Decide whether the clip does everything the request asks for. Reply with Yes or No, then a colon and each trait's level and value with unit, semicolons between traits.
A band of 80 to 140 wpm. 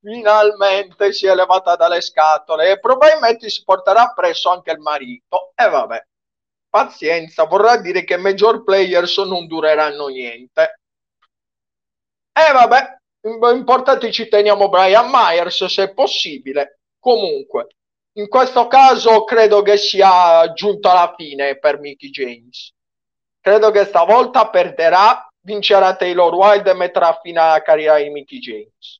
Yes: average, 135 wpm